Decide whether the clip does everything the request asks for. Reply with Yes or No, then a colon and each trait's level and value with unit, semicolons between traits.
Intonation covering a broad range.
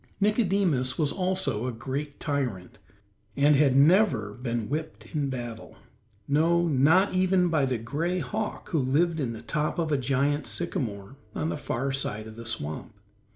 Yes: wide, 5.9 semitones